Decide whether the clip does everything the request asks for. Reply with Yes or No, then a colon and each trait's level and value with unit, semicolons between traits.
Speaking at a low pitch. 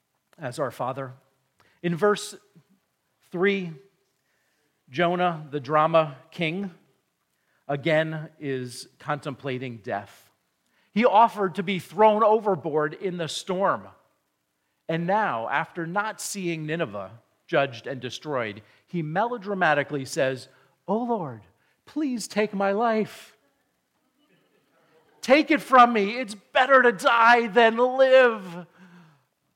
No: medium, 175 Hz